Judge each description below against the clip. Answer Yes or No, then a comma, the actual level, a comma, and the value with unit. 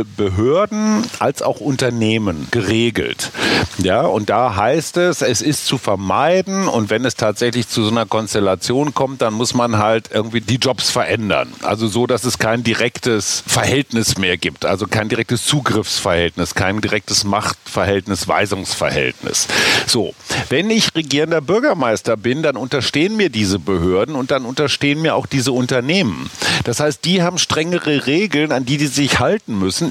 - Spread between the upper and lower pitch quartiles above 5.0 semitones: Yes, wide, 5.5 semitones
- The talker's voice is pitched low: Yes, low, 120 Hz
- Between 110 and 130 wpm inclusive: No, average, 155 wpm